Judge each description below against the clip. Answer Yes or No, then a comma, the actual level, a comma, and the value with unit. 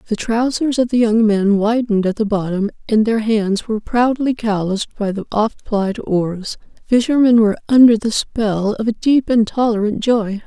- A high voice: Yes, high, 220 Hz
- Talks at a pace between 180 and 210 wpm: Yes, average, 185 wpm